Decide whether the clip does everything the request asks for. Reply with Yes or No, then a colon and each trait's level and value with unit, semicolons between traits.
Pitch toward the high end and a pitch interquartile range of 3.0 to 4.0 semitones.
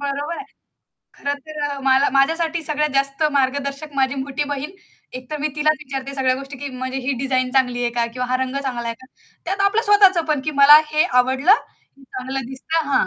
No: very high, 275 Hz; narrow, 2.6 semitones